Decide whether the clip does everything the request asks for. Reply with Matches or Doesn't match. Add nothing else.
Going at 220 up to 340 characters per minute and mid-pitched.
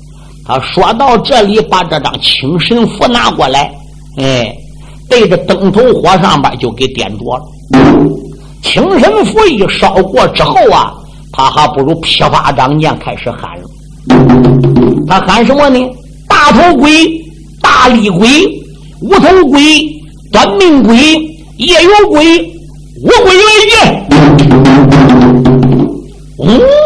Doesn't match